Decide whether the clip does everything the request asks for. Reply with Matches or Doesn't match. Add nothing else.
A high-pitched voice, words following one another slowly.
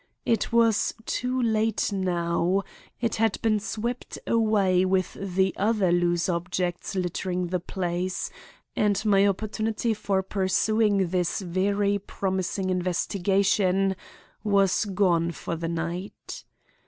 Matches